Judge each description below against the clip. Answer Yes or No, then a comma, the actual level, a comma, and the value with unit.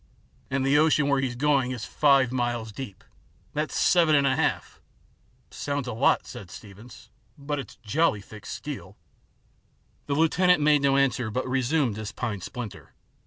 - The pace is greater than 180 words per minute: No, average, 165 wpm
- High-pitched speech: No, low, 130 Hz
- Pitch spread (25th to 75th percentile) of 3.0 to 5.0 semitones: Yes, average, 3.8 semitones